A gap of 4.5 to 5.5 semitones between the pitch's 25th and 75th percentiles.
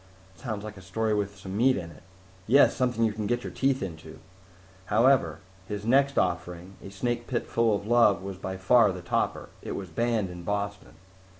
No: average, 4.0 semitones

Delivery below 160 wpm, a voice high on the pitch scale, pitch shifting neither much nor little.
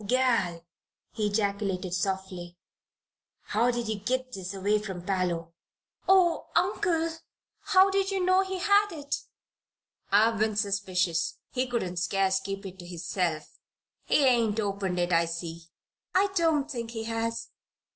No: slow, 135 wpm; high, 210 Hz; wide, 6.0 semitones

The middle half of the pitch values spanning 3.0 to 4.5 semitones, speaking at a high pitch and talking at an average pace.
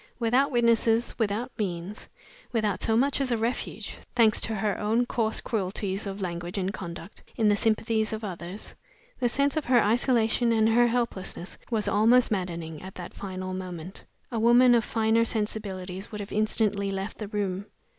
Yes: average, 3.3 semitones; high, 215 Hz; average, 170 wpm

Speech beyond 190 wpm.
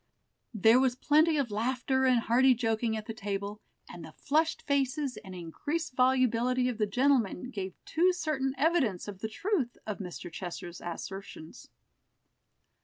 No: average, 150 wpm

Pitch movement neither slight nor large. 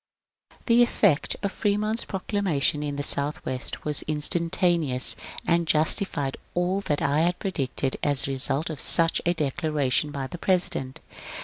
Yes: average, 4.1 semitones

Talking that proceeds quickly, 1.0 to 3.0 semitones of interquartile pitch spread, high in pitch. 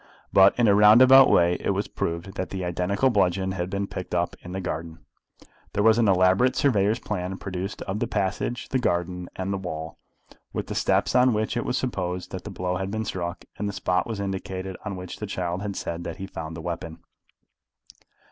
No: fast, 215 wpm; average, 2.7 semitones; very low, 95 Hz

